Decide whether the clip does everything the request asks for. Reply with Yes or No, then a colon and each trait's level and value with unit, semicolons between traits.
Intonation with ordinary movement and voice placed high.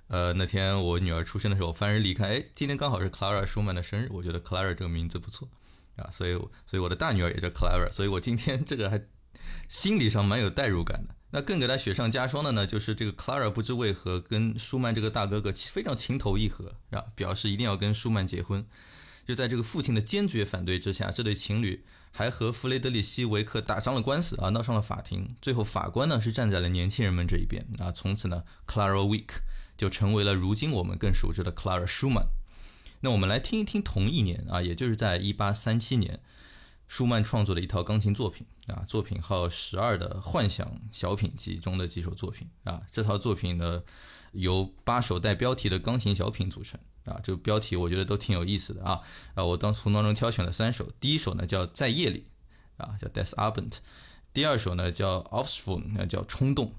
No: average, 3.6 semitones; low, 105 Hz